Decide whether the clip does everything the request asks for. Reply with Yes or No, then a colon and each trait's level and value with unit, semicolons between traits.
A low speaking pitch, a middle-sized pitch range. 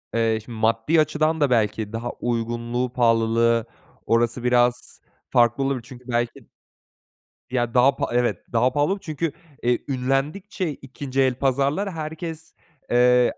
Yes: low, 125 Hz; average, 3.1 semitones